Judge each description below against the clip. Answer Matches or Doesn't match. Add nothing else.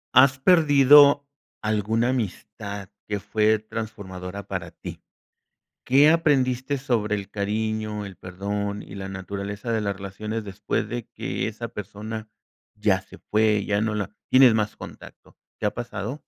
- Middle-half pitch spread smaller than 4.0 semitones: Matches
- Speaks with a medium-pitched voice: Doesn't match